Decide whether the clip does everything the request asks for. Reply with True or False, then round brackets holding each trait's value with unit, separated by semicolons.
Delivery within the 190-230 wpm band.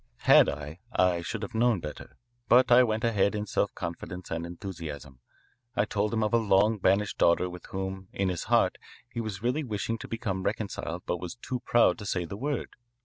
True (200 wpm)